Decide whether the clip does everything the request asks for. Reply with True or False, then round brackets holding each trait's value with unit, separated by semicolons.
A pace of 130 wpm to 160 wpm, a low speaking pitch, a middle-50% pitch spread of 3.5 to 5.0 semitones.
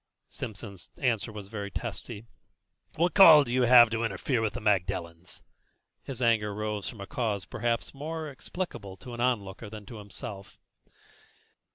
True (150 wpm; 110 Hz; 3.8 semitones)